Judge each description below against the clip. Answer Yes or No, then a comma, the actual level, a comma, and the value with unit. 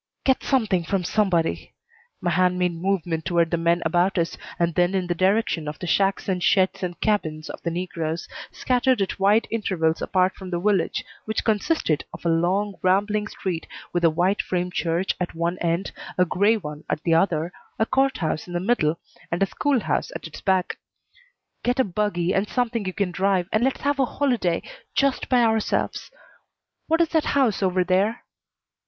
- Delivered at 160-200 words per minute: Yes, average, 190 wpm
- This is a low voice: No, medium, 185 Hz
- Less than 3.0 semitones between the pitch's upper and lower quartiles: No, average, 3.7 semitones